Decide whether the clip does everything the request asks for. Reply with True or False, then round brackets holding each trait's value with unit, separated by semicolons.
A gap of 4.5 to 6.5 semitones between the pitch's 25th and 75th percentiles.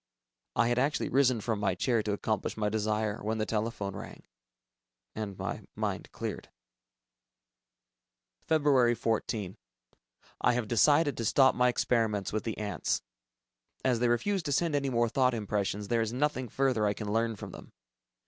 False (3.3 semitones)